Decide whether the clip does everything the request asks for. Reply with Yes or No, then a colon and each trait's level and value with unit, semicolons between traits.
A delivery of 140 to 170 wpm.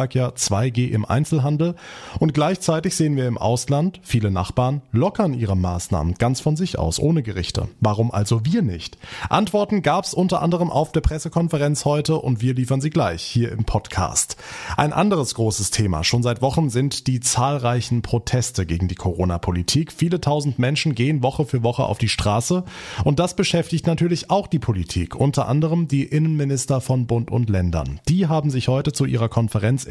No: average, 180 wpm